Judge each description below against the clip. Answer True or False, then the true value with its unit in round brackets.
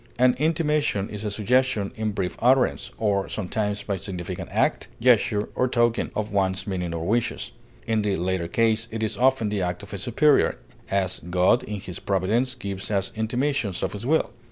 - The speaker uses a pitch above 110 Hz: False (105 Hz)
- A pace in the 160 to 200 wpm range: True (180 wpm)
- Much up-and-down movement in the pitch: False (3.8 semitones)